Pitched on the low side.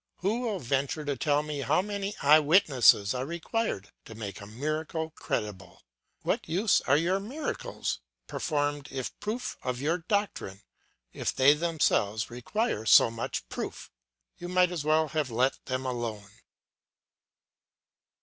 No: medium, 150 Hz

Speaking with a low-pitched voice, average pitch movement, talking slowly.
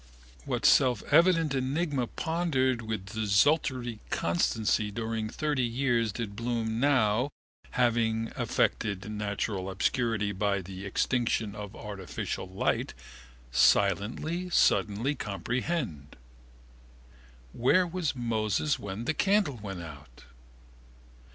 Yes: low, 115 Hz; average, 4.6 semitones; slow, 95 wpm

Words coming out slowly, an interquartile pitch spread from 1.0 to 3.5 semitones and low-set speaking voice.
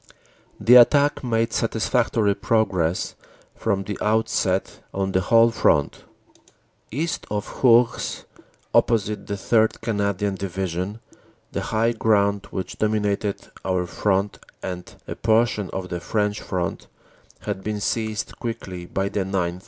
Yes: slow, 125 wpm; average, 2.9 semitones; low, 105 Hz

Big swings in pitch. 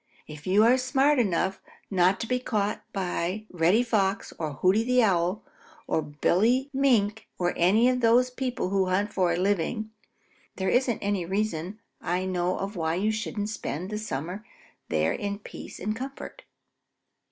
No: average, 4.1 semitones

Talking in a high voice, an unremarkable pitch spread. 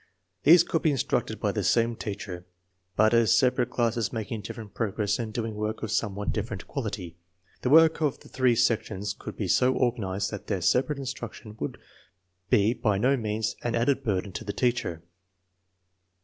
No: low, 110 Hz; average, 3.3 semitones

